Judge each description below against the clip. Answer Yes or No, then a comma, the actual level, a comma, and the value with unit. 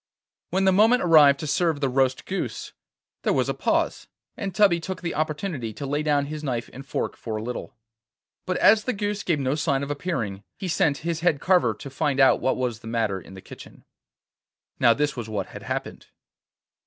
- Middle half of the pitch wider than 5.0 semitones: Yes, wide, 5.5 semitones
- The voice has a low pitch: No, medium, 145 Hz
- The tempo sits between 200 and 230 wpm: Yes, fast, 205 wpm